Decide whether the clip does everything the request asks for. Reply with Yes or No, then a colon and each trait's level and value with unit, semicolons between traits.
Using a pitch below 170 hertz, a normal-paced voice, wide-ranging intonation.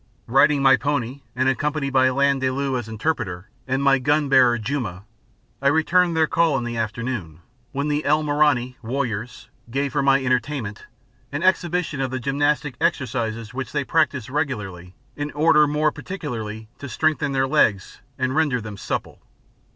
No: low, 135 Hz; average, 155 wpm; average, 3.7 semitones